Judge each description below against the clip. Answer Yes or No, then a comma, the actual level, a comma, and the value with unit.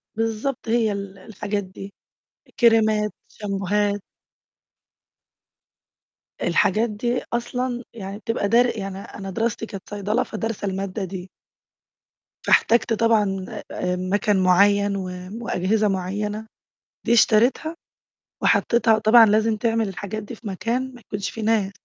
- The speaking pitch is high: Yes, high, 210 Hz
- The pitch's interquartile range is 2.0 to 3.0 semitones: Yes, narrow, 2.4 semitones